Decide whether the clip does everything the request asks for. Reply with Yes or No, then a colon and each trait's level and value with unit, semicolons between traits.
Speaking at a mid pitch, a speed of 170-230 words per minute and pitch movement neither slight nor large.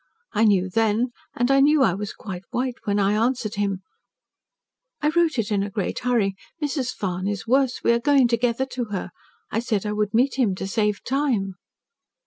No: high, 225 Hz; average, 195 wpm; average, 4.1 semitones